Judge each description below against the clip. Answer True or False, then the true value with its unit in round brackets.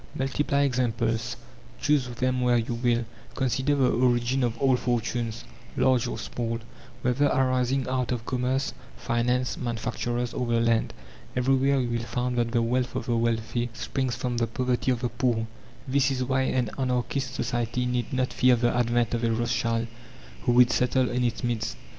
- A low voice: True (125 Hz)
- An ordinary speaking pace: True (170 wpm)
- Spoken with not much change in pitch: True (1.5 semitones)